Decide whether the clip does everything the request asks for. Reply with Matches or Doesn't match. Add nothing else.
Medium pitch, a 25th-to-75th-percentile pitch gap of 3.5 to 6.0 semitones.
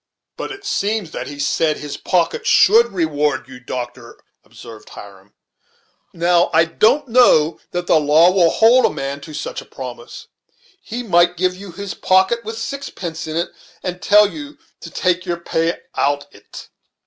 Matches